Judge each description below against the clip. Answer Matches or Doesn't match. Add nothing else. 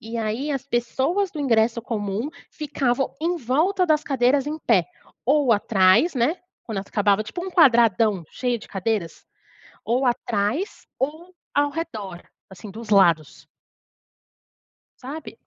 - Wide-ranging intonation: Matches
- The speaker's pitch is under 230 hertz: Doesn't match